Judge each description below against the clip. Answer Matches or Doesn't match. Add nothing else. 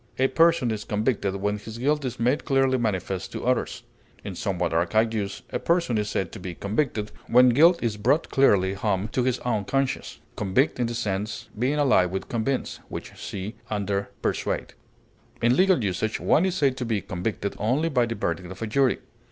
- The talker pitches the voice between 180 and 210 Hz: Doesn't match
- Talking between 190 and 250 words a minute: Matches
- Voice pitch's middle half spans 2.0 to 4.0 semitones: Doesn't match